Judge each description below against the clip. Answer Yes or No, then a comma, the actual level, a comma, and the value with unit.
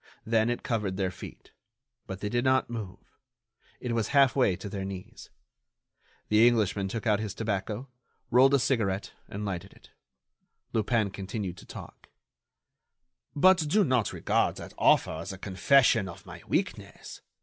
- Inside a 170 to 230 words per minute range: No, average, 155 wpm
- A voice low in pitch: Yes, low, 110 Hz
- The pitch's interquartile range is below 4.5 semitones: Yes, average, 3.8 semitones